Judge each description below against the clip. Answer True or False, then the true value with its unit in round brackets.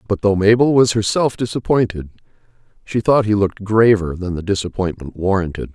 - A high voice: False (100 Hz)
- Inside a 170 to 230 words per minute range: False (155 wpm)